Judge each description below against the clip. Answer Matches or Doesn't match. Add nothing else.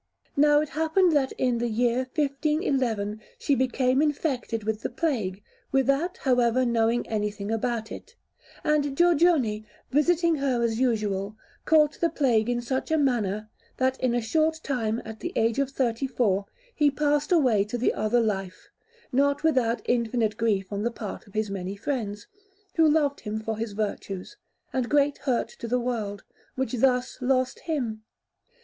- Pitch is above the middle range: Matches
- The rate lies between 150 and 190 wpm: Matches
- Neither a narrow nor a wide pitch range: Matches